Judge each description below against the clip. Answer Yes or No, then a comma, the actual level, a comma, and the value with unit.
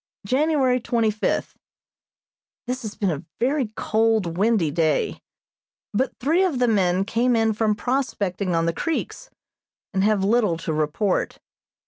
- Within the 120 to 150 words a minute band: Yes, average, 140 wpm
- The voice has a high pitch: Yes, high, 220 Hz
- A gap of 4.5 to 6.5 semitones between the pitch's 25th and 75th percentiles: Yes, average, 5.1 semitones